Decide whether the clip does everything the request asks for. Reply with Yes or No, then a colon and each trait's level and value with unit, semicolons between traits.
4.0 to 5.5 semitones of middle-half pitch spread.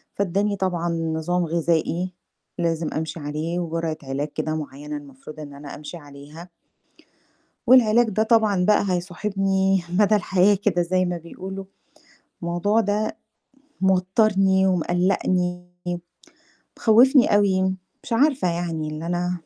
No: average, 3.3 semitones